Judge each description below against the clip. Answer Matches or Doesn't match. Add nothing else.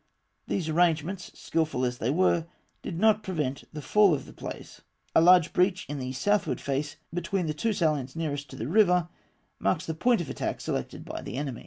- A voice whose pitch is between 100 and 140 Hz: Doesn't match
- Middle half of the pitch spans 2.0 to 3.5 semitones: Doesn't match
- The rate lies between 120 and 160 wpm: Doesn't match